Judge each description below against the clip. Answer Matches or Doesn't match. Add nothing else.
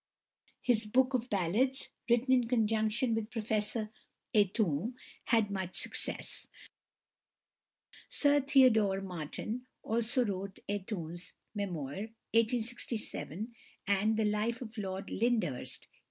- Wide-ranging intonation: Doesn't match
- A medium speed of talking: Doesn't match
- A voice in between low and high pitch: Doesn't match